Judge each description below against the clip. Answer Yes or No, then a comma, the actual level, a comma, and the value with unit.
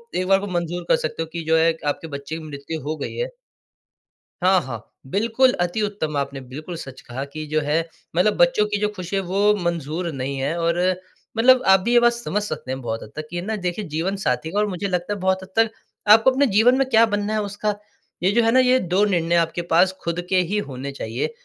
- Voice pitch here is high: No, medium, 180 Hz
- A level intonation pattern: No, average, 5.1 semitones